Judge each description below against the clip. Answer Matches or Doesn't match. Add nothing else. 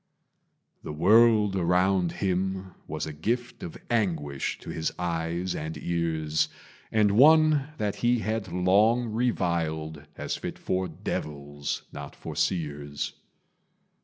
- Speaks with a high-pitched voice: Doesn't match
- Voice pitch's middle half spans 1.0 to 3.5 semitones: Doesn't match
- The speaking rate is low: Matches